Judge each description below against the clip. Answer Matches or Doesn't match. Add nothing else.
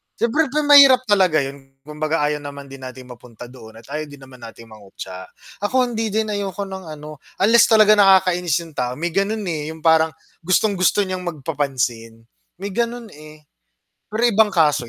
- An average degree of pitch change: Doesn't match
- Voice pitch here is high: Doesn't match